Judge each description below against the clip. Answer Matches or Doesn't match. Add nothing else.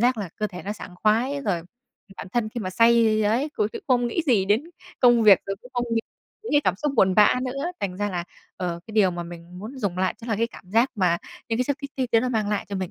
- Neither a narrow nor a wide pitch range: Matches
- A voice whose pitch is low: Doesn't match